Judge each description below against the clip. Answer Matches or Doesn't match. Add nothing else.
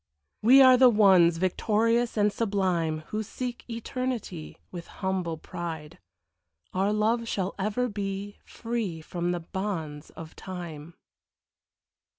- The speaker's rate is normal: Doesn't match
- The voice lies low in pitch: Doesn't match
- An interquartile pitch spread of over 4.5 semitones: Matches